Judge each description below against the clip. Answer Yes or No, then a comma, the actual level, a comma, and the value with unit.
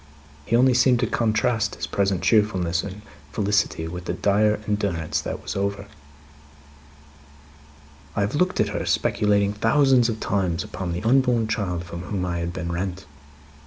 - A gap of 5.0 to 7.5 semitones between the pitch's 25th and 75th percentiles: No, average, 3.7 semitones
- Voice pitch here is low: Yes, low, 100 Hz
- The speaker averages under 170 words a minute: Yes, average, 160 wpm